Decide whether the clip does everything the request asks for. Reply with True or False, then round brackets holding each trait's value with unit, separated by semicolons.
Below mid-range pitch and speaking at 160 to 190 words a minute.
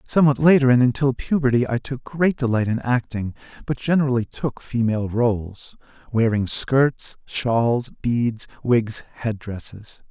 False (120 Hz; 135 wpm)